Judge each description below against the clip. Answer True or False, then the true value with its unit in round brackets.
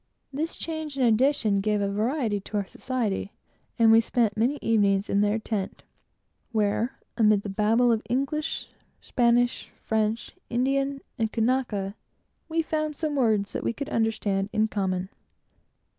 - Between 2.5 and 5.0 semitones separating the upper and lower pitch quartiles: True (4.1 semitones)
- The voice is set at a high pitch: True (225 Hz)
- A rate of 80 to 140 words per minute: True (135 wpm)